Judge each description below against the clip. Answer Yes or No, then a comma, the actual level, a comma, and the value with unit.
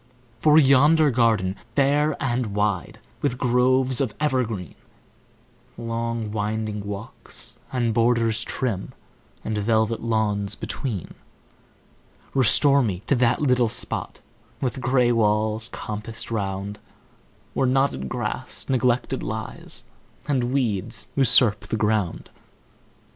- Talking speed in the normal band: No, slow, 105 wpm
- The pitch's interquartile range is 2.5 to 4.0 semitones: Yes, average, 3.4 semitones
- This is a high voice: No, low, 115 Hz